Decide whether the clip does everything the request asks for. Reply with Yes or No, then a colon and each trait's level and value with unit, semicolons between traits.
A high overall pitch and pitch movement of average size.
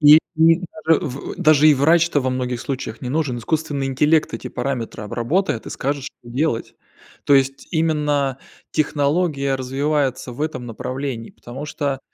No: medium, 140 Hz; average, 3.2 semitones